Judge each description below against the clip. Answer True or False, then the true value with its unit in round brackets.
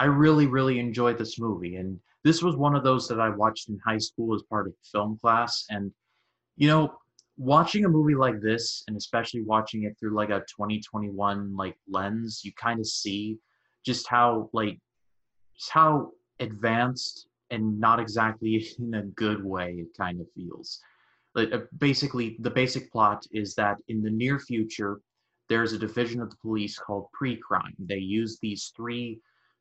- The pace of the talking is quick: False (175 wpm)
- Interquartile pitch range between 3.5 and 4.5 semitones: False (2.5 semitones)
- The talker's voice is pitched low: True (110 Hz)